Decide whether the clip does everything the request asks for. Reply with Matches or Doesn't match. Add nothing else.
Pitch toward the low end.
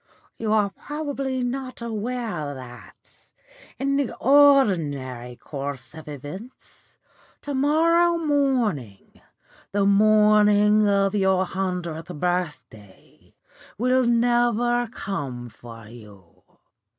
Doesn't match